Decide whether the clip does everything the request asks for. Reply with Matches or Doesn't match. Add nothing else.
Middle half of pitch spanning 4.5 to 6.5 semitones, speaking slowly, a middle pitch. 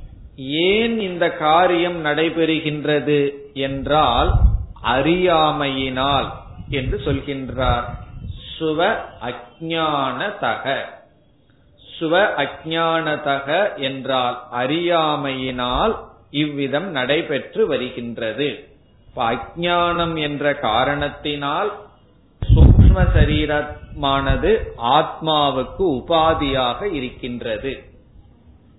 Doesn't match